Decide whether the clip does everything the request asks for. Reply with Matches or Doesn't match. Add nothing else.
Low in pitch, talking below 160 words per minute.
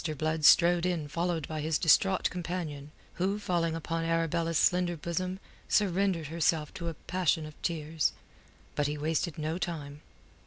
Doesn't match